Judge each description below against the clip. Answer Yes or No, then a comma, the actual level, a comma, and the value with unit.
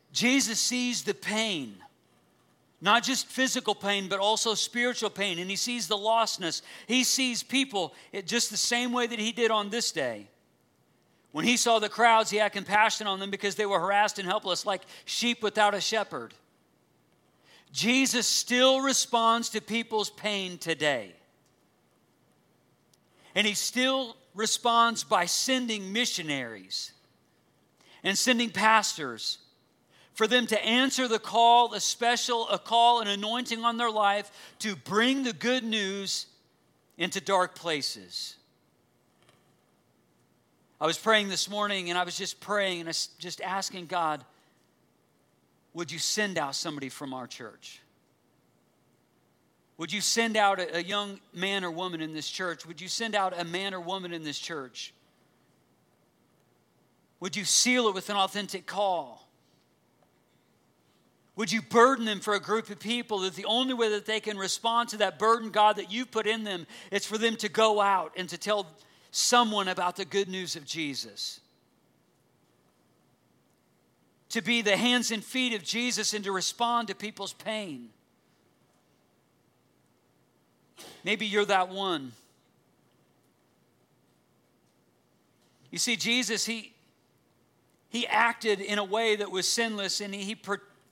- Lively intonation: No, average, 3.6 semitones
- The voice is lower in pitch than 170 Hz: No, high, 210 Hz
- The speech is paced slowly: No, average, 145 wpm